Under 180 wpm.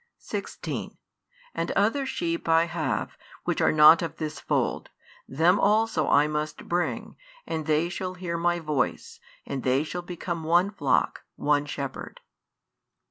Yes: average, 140 wpm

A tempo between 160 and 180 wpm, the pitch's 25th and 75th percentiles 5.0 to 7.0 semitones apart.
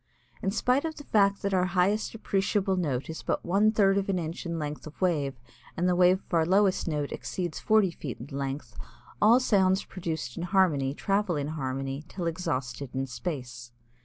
No: average, 190 wpm; average, 5.3 semitones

